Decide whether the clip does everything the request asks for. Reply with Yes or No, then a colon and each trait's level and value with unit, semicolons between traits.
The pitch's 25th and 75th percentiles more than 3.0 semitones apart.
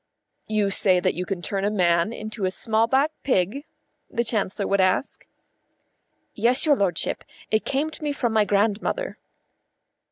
Yes: average, 4.2 semitones